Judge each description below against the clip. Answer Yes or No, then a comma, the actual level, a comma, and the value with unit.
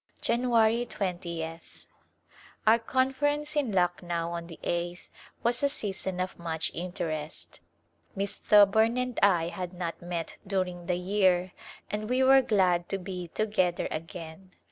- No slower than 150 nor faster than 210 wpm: No, average, 140 wpm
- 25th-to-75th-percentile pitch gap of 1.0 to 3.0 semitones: No, average, 4.3 semitones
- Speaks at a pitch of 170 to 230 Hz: Yes, medium, 185 Hz